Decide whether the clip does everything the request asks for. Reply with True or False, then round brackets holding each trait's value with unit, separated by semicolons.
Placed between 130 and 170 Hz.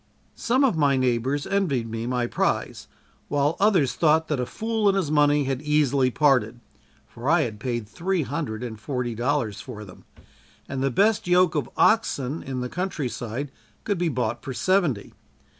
True (140 Hz)